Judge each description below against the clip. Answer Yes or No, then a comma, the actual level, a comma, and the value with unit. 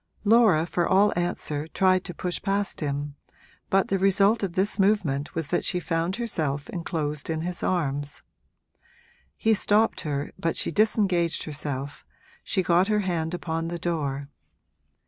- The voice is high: No, medium, 175 Hz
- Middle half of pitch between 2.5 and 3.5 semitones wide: No, average, 4.2 semitones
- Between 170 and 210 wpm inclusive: No, average, 150 wpm